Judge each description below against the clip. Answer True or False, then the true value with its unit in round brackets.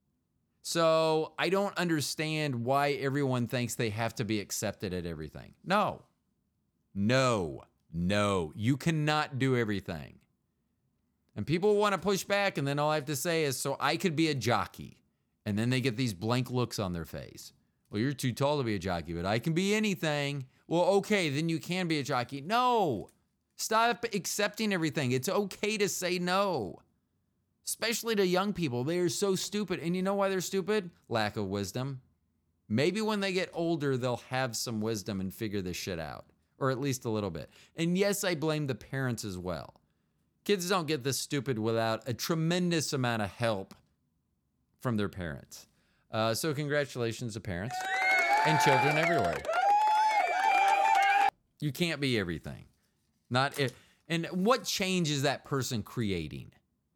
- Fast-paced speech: False (170 wpm)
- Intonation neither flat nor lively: False (8.5 semitones)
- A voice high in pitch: False (140 Hz)